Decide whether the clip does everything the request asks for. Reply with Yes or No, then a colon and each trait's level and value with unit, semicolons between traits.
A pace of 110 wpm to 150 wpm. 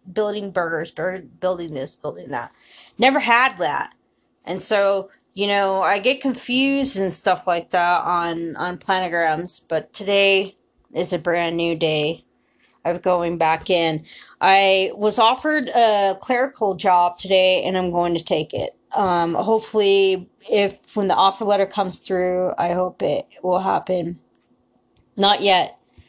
Yes: average, 145 wpm